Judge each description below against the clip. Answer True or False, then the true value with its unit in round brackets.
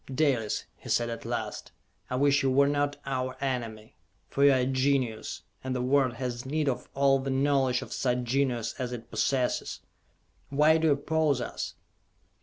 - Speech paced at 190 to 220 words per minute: False (180 wpm)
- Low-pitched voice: True (130 Hz)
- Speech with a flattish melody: True (2.1 semitones)